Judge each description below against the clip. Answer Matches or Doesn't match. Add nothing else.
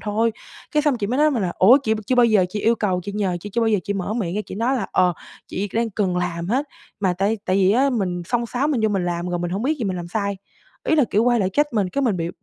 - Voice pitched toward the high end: Matches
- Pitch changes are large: Doesn't match